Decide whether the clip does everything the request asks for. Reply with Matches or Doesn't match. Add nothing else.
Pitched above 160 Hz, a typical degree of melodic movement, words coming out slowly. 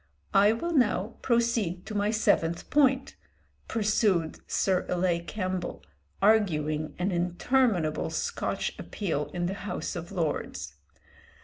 Matches